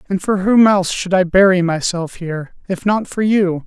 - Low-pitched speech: No, medium, 185 Hz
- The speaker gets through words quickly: Yes, fast, 215 wpm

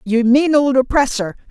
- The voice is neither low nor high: No, very high, 260 Hz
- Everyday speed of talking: Yes, average, 160 wpm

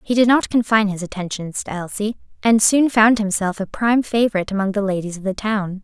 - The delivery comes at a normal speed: No, fast, 215 wpm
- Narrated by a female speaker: Yes, female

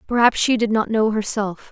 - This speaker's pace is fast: Yes, fast, 210 wpm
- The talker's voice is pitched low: No, high, 220 Hz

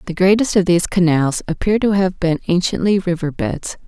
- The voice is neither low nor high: Yes, medium, 180 Hz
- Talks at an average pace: Yes, average, 185 wpm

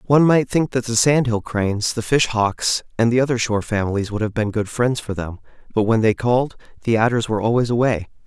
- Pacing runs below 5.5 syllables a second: No, 5.9 syllables/s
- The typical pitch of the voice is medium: No, low, 115 Hz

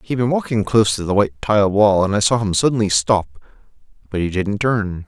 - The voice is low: Yes, low, 105 Hz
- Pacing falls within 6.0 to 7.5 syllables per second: Yes, 6.1 syllables/s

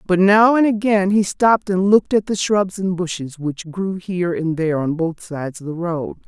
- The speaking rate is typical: No, fast, 230 wpm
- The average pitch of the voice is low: No, medium, 185 Hz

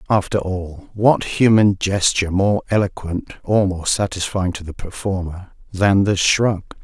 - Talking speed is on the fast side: No, average, 140 wpm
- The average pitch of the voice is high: No, very low, 95 Hz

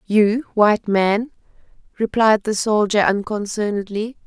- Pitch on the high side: Yes, high, 210 Hz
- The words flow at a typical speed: No, slow, 100 wpm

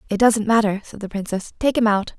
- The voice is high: Yes, high, 215 Hz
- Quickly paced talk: Yes, fast, 245 wpm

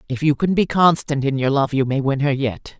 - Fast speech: Yes, fast, 280 wpm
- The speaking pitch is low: No, medium, 145 Hz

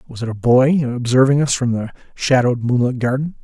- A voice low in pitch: Yes, low, 125 Hz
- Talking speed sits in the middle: Yes, average, 190 wpm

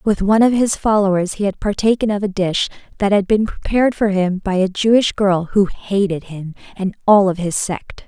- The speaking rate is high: Yes, fast, 215 wpm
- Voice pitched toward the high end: Yes, high, 200 Hz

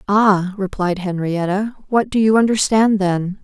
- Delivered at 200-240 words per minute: No, average, 140 wpm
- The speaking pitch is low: No, high, 200 Hz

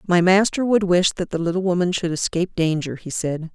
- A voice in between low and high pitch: Yes, medium, 180 Hz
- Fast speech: Yes, fast, 220 wpm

